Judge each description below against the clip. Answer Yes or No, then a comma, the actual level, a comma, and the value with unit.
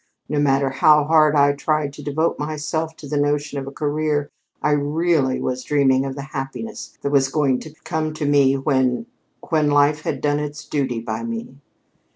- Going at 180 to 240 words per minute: Yes, average, 190 wpm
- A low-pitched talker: No, medium, 145 Hz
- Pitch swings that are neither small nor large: No, narrow, 2.0 semitones